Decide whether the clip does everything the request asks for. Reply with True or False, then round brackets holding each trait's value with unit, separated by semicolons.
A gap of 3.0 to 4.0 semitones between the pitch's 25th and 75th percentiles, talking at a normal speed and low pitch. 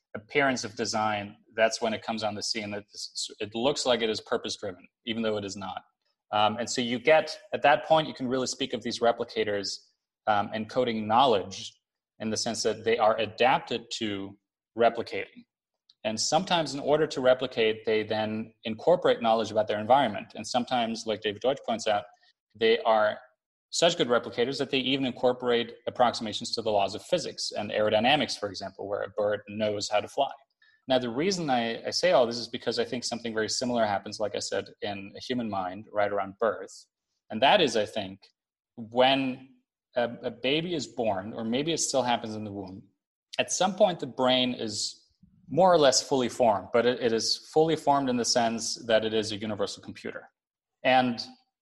True (3.3 semitones; 195 wpm; 115 Hz)